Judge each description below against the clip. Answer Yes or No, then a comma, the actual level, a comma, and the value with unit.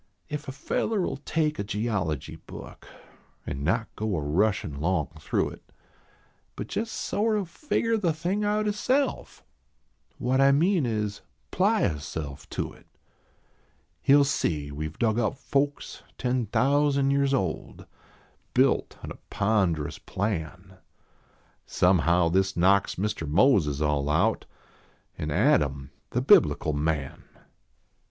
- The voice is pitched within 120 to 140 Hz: No, low, 105 Hz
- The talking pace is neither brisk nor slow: No, slow, 130 wpm